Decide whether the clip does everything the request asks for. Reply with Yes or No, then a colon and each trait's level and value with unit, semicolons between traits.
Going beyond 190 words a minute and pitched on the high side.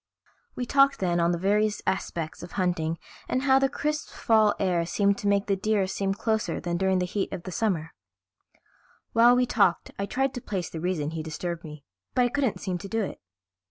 Yes: fast, 205 wpm; high, 195 Hz